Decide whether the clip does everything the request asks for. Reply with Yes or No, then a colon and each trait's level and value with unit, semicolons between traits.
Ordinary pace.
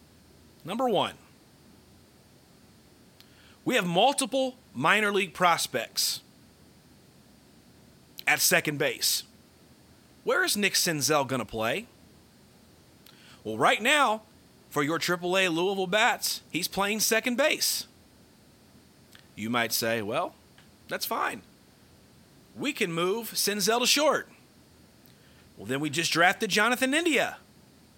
No: slow, 105 wpm